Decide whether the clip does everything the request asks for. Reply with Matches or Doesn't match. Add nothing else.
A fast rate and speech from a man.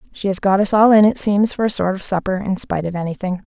Doesn't match